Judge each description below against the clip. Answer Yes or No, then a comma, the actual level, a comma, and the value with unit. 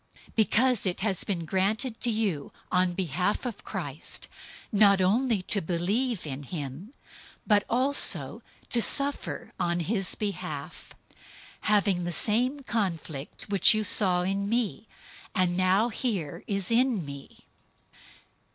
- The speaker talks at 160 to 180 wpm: No, slow, 135 wpm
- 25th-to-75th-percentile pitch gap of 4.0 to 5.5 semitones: Yes, average, 4.3 semitones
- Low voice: No, high, 200 Hz